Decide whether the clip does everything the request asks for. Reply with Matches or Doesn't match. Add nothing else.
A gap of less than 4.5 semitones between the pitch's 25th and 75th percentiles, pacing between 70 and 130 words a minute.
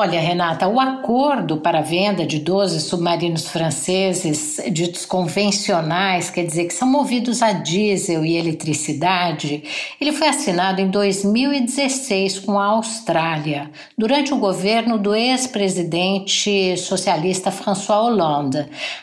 Matches